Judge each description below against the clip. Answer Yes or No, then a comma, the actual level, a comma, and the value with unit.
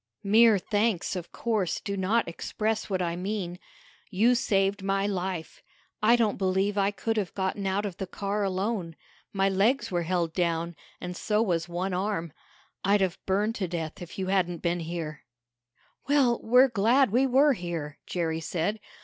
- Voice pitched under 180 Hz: No, high, 195 Hz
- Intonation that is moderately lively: Yes, average, 3.3 semitones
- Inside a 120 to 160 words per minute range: No, average, 170 wpm